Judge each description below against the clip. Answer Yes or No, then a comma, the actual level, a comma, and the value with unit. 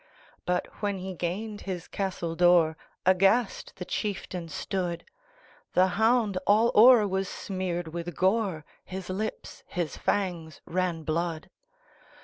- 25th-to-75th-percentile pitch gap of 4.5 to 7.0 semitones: No, average, 2.9 semitones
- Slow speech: Yes, slow, 110 wpm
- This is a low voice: No, medium, 185 Hz